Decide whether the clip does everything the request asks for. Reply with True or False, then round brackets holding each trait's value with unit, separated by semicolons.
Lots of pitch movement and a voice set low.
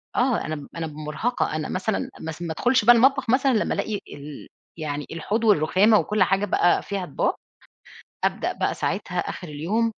False (6.4 semitones; 190 Hz)